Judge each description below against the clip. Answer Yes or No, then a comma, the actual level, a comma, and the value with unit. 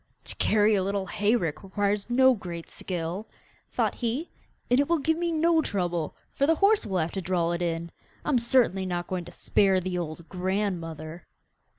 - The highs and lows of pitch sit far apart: Yes, wide, 5.7 semitones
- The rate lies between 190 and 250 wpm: Yes, average, 195 wpm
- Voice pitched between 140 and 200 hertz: Yes, high, 190 Hz